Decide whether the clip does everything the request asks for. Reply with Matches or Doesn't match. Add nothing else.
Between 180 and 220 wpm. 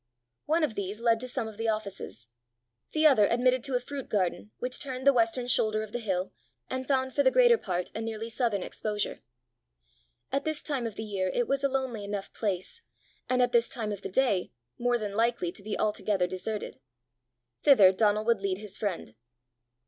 Matches